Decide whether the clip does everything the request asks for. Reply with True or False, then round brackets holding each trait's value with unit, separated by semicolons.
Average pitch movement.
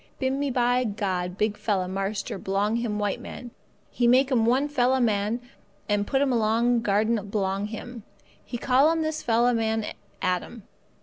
True (3.5 semitones)